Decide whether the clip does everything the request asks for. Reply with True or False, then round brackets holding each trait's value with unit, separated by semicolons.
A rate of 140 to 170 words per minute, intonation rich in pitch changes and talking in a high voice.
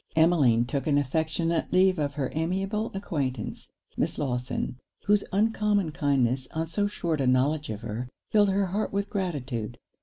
False (155 wpm; 6.8 semitones; 155 Hz)